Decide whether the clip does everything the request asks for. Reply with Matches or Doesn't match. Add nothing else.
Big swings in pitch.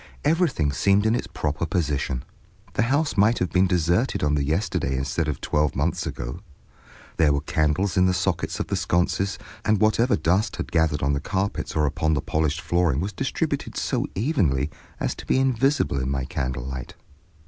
Matches